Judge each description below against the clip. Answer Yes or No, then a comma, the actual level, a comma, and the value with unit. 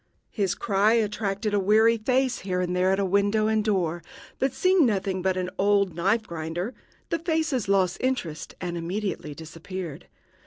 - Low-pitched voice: No, high, 200 Hz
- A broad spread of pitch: No, average, 3.3 semitones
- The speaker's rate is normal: Yes, average, 160 wpm